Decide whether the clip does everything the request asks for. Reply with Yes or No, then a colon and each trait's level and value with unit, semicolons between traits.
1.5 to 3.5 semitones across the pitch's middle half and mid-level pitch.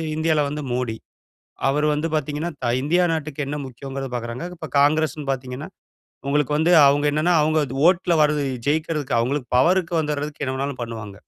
Yes: average, 2.8 semitones; medium, 150 Hz